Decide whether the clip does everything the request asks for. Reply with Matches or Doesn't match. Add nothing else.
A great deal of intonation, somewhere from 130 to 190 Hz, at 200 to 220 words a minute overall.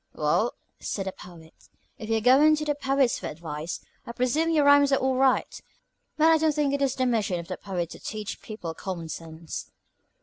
Doesn't match